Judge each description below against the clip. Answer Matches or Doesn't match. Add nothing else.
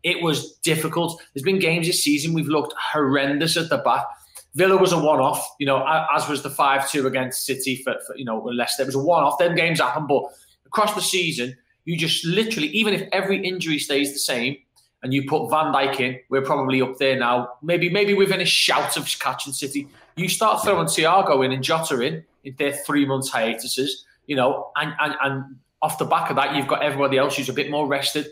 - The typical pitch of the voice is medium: Matches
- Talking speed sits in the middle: Doesn't match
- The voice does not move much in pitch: Doesn't match